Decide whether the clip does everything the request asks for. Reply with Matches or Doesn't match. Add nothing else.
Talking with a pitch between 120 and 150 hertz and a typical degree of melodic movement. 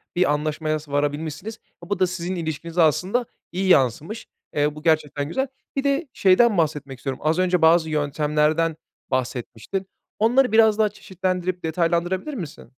Doesn't match